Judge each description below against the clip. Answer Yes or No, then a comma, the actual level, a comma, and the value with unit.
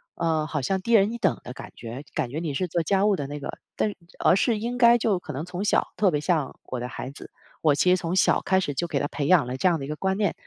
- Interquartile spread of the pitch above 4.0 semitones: Yes, average, 5.0 semitones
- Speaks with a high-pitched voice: No, medium, 170 Hz